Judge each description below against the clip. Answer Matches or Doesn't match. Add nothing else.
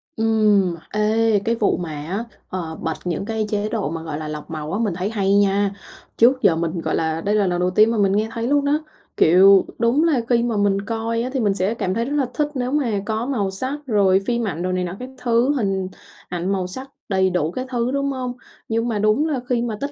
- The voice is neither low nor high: Doesn't match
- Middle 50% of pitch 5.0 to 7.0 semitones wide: Doesn't match